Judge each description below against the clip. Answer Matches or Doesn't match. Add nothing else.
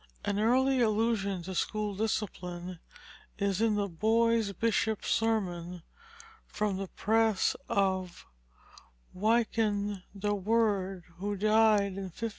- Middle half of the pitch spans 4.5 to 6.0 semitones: Doesn't match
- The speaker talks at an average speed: Doesn't match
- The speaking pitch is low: Doesn't match